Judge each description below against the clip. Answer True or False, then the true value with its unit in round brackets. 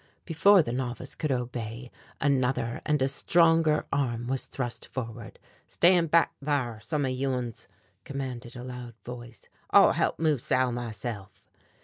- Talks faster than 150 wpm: False (145 wpm)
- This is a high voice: False (130 Hz)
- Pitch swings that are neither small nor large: True (3.3 semitones)